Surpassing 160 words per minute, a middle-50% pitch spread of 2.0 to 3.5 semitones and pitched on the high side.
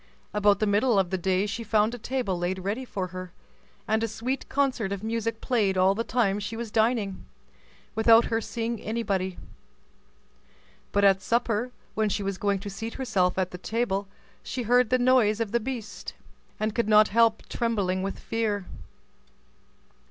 Yes: average, 170 wpm; average, 2.9 semitones; high, 215 Hz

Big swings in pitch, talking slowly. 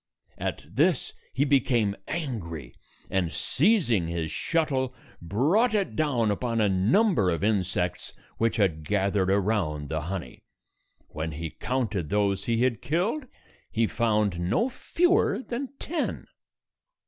Yes: wide, 7.6 semitones; slow, 125 wpm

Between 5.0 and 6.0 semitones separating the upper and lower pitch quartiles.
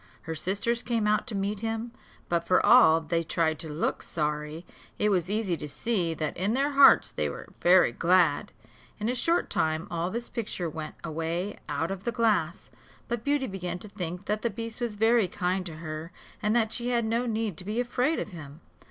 Yes: wide, 5.5 semitones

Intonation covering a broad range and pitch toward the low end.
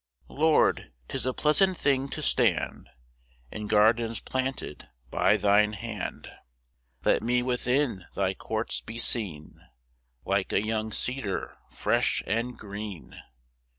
No: average, 3.6 semitones; low, 110 Hz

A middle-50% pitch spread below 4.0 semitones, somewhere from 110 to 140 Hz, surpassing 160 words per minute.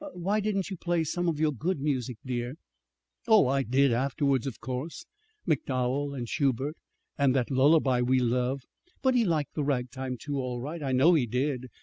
Yes: average, 3.6 semitones; low, 135 Hz; average, 185 wpm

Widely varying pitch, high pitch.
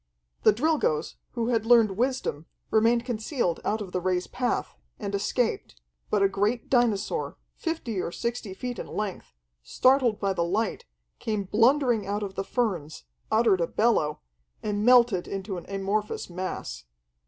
No: average, 3.8 semitones; high, 215 Hz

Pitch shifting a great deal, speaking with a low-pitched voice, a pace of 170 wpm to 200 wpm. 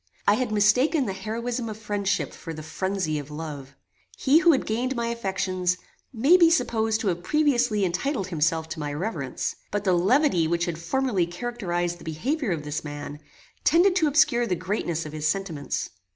No: wide, 6.4 semitones; high, 195 Hz; average, 180 wpm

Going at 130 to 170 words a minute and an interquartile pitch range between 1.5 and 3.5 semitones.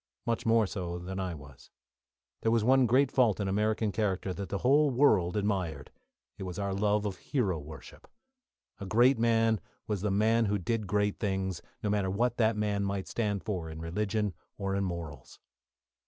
No: average, 185 wpm; average, 3.0 semitones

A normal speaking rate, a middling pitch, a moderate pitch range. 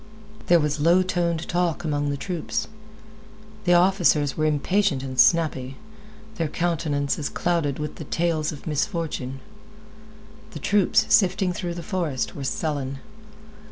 No: slow, 130 wpm; medium, 165 Hz; average, 3.4 semitones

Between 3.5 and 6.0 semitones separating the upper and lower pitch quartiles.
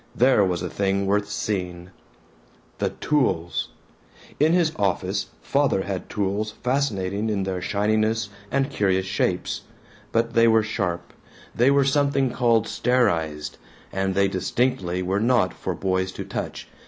Yes: average, 4.4 semitones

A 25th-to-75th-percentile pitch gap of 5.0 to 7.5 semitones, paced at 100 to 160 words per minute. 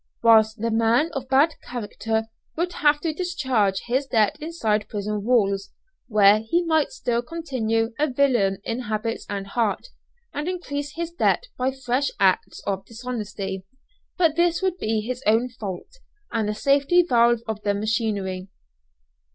Yes: average, 5.3 semitones; average, 150 wpm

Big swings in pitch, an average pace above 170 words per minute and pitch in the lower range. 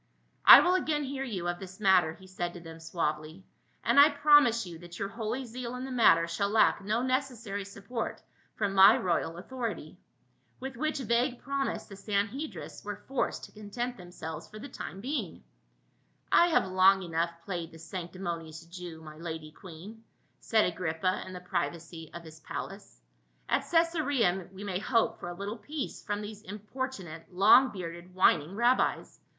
No: wide, 5.7 semitones; average, 180 wpm; high, 195 Hz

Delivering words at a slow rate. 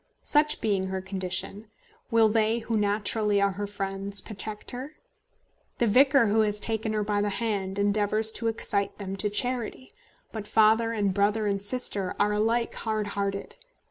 No: average, 165 wpm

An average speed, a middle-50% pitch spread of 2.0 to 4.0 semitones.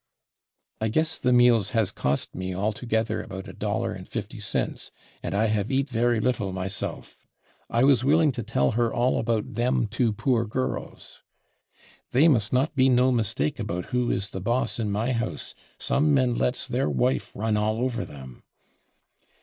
Yes: average, 165 wpm; average, 3.3 semitones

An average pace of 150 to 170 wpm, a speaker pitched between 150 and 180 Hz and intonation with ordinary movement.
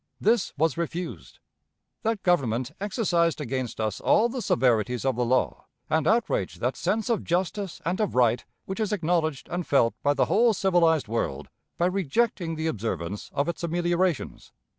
No: average, 160 wpm; medium, 170 Hz; wide, 6.7 semitones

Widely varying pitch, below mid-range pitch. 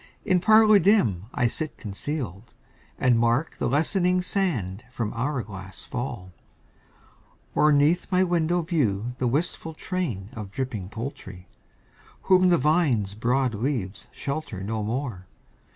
Yes: wide, 7.7 semitones; low, 130 Hz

